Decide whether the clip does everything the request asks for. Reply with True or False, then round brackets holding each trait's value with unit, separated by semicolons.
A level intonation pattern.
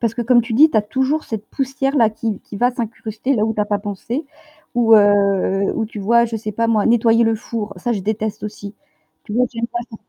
True (2.3 semitones)